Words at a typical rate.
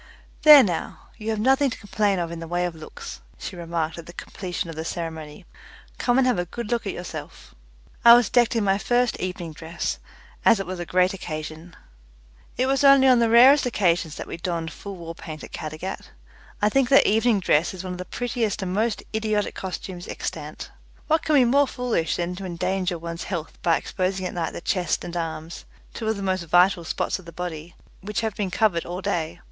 No: fast, 215 wpm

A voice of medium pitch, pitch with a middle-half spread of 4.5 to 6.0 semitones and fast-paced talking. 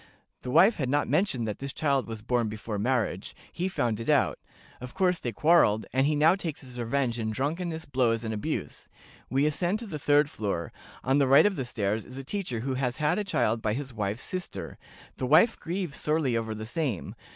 No: low, 130 Hz; average, 5.2 semitones; fast, 215 wpm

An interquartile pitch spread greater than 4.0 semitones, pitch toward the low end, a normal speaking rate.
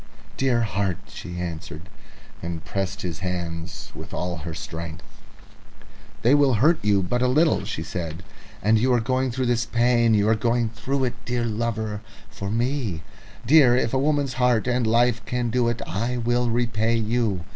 Yes: average, 4.4 semitones; low, 115 Hz; average, 170 wpm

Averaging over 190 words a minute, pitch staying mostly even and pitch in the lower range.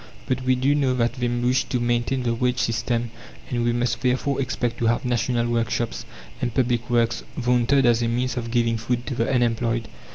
Yes: average, 200 wpm; narrow, 1.3 semitones; low, 120 Hz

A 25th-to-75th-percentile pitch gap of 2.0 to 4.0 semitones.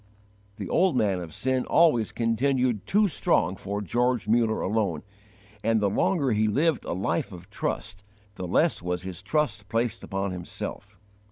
No: average, 5.0 semitones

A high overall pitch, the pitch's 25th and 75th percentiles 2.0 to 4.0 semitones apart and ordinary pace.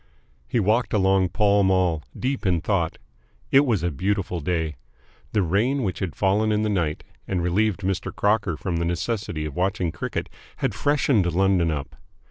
No: very low, 95 Hz; average, 3.6 semitones; average, 170 wpm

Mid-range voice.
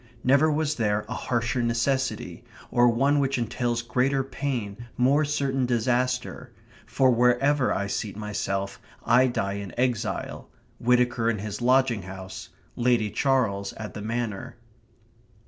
No: low, 120 Hz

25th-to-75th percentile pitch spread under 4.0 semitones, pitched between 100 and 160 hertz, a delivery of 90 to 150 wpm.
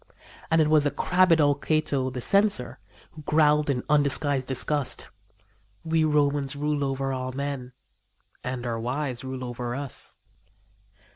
Yes: narrow, 2.6 semitones; medium, 140 Hz; average, 140 wpm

